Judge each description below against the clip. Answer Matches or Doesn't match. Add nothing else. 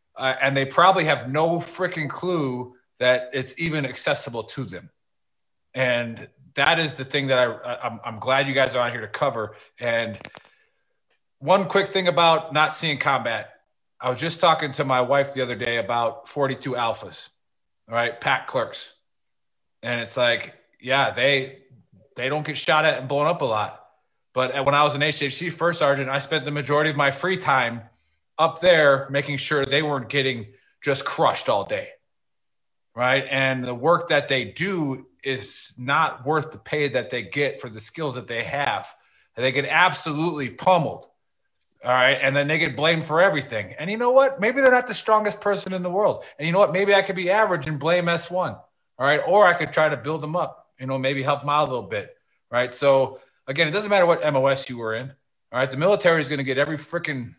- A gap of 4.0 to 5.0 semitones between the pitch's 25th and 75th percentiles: Matches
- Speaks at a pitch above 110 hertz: Matches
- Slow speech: Doesn't match